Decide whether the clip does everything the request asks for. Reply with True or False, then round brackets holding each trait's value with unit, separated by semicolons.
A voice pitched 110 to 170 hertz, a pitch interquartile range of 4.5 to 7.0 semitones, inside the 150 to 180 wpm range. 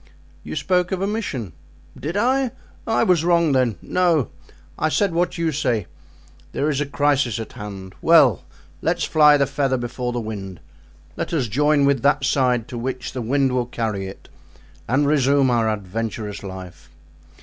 True (135 Hz; 5.1 semitones; 165 wpm)